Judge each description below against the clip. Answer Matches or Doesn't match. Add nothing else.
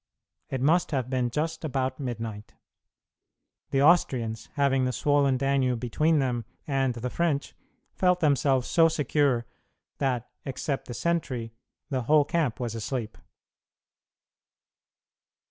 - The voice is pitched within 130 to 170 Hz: Matches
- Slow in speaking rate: Matches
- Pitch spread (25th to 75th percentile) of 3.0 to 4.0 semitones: Matches